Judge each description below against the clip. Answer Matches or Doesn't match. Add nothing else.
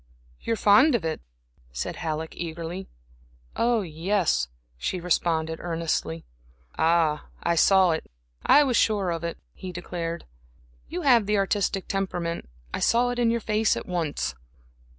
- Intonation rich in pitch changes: Doesn't match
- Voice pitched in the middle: Matches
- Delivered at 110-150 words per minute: Matches